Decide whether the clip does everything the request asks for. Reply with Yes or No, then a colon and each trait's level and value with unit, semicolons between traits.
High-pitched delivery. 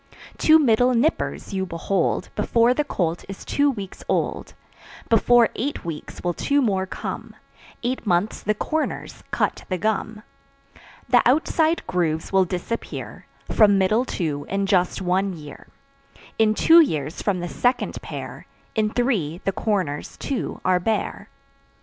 Yes: high, 205 Hz